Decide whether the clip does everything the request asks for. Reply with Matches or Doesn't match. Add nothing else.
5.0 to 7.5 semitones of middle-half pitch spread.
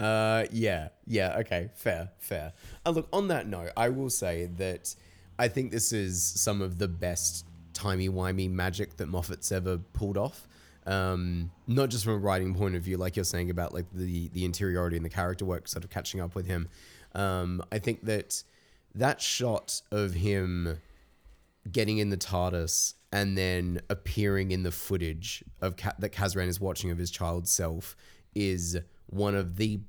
Doesn't match